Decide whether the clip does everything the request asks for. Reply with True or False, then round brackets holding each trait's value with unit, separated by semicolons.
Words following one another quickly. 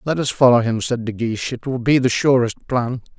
True (245 wpm)